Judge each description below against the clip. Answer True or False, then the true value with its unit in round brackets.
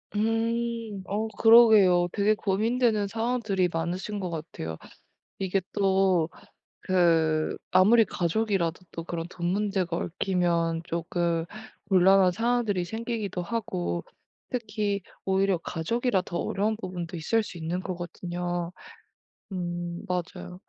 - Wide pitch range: False (3.8 semitones)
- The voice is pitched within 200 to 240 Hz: False (185 Hz)